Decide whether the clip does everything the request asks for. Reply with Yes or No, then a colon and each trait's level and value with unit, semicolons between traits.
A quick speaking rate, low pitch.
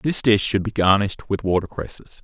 Yes: fast, 215 wpm; low, 105 Hz